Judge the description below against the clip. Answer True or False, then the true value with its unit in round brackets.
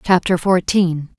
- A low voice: False (175 Hz)